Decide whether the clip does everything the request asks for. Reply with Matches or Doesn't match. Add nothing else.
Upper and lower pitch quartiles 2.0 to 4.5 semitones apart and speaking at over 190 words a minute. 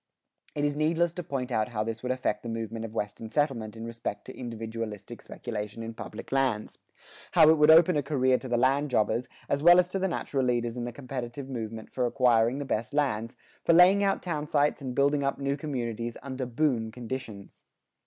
Matches